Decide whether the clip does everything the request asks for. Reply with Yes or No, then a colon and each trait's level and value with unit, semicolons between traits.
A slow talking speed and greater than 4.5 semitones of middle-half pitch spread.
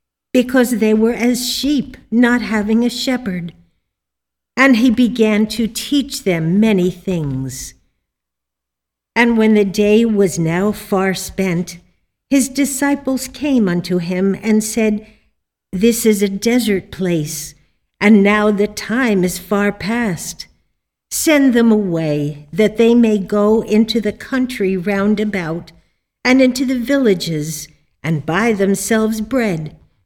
Yes: slow, 130 wpm; average, 5.0 semitones